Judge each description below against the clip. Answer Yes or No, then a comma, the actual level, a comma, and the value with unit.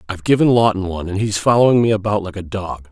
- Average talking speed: No, fast, 245 wpm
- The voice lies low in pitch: Yes, low, 100 Hz